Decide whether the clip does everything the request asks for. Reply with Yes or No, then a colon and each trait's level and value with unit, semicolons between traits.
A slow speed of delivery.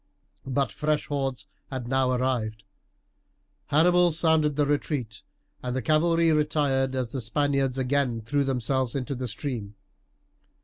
Yes: slow, 130 wpm